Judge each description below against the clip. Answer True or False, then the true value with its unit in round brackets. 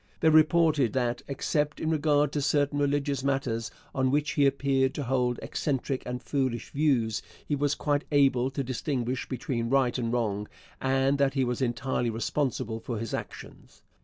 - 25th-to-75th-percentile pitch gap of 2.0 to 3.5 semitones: True (2.9 semitones)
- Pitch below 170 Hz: True (135 Hz)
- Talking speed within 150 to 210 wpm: True (165 wpm)